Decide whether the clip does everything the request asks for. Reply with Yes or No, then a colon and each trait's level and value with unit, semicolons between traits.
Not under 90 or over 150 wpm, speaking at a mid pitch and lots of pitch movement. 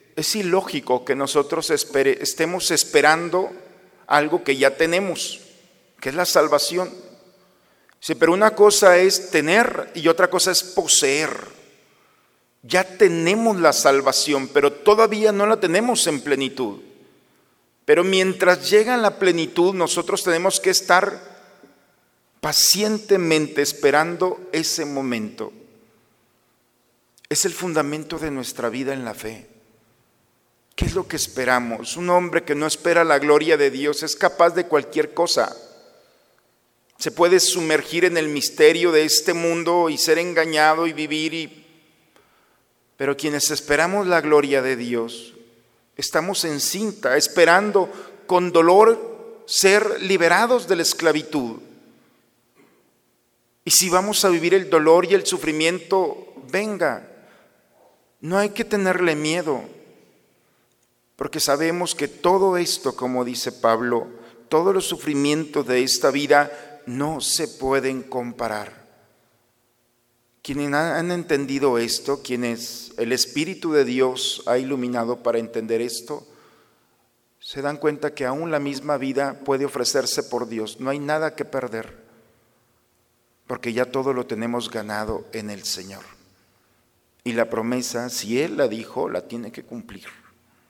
Yes: average, 130 wpm; medium, 155 Hz; wide, 6.0 semitones